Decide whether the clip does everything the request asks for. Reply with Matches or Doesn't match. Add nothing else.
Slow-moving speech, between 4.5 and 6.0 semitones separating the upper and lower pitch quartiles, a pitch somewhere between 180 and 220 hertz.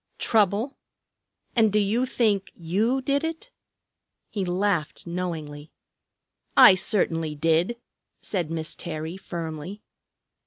Matches